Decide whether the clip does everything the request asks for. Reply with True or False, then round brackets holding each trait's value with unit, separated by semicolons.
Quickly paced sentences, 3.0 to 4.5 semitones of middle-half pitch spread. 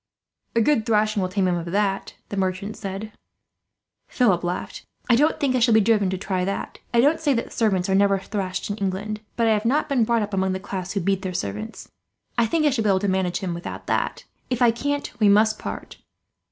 True (230 wpm; 3.4 semitones)